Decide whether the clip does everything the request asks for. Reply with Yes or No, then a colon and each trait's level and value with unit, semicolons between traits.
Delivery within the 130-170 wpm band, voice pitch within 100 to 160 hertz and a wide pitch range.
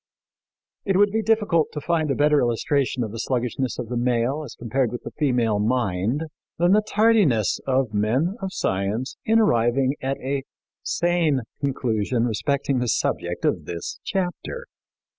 Yes: average, 160 wpm; low, 135 Hz; wide, 6.2 semitones